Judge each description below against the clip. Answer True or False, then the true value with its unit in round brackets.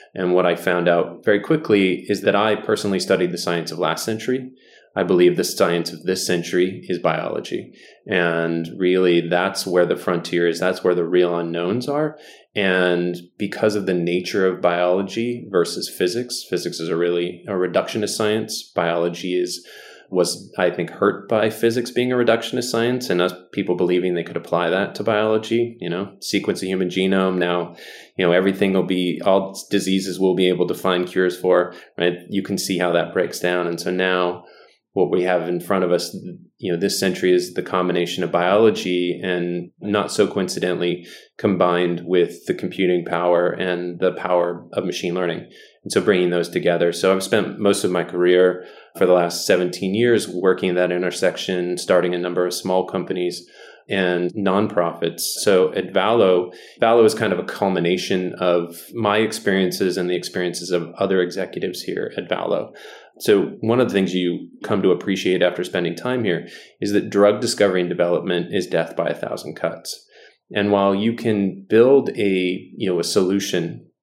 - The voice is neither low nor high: False (90 Hz)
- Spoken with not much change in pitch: True (1.9 semitones)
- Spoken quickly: False (180 wpm)